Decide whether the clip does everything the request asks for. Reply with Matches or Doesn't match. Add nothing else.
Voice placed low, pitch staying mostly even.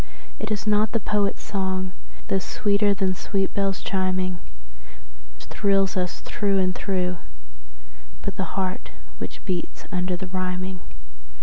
Doesn't match